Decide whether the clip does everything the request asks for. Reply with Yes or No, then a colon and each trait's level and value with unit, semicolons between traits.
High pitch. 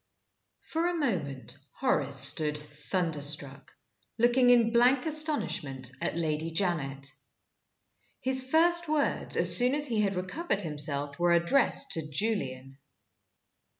No: medium, 175 Hz